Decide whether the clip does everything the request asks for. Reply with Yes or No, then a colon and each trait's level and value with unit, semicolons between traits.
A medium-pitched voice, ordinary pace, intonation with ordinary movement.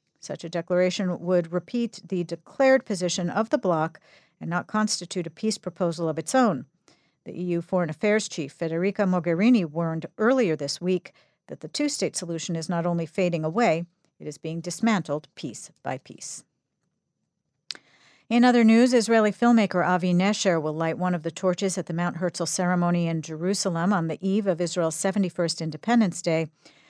Yes: medium, 180 Hz; average, 170 wpm; average, 3.4 semitones